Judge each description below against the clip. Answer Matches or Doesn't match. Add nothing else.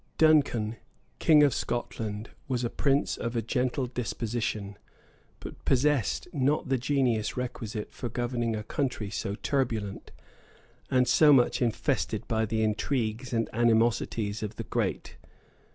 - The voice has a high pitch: Doesn't match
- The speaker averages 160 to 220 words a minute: Doesn't match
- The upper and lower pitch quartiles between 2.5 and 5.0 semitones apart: Matches